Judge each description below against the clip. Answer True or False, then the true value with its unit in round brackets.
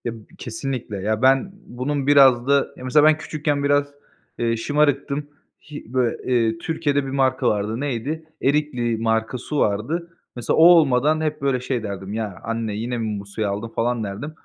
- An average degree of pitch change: True (4.3 semitones)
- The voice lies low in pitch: True (125 Hz)